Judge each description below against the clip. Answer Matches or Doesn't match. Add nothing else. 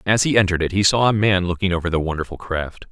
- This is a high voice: Doesn't match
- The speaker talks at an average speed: Doesn't match